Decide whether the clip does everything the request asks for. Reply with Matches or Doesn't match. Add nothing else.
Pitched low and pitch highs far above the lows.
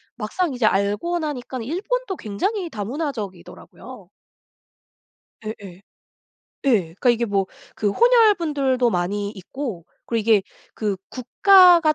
Doesn't match